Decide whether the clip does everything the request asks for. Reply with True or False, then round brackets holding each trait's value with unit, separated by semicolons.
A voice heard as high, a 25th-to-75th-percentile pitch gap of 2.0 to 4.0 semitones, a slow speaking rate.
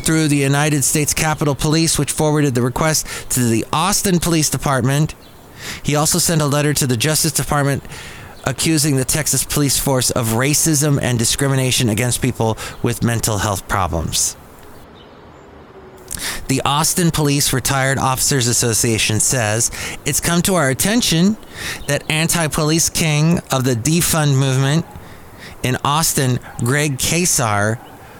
False (145 Hz; 3.6 semitones; 130 wpm)